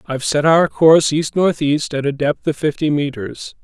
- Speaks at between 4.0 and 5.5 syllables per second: Yes, 4.9 syllables/s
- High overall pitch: No, medium, 150 Hz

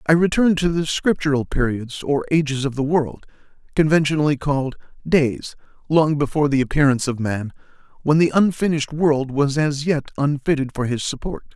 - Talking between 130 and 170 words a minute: Yes, average, 160 wpm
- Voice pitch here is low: No, medium, 145 Hz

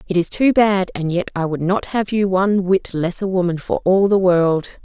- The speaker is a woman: Yes, female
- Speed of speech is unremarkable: No, fast, 250 wpm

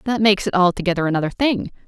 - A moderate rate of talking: Yes, average, 190 wpm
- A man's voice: No, female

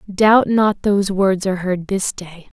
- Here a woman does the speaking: Yes, female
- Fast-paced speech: No, average, 185 wpm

